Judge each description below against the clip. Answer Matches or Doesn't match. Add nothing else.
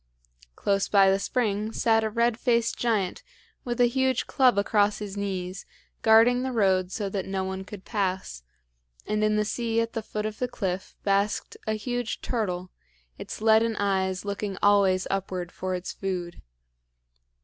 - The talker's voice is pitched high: Matches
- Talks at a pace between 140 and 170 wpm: Matches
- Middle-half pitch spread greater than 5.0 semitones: Doesn't match